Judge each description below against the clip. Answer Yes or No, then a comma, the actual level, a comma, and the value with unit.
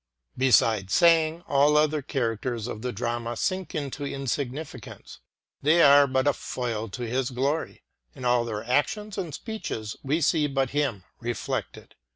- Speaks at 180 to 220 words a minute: No, average, 150 wpm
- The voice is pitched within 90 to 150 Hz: Yes, low, 135 Hz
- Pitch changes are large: No, average, 4.0 semitones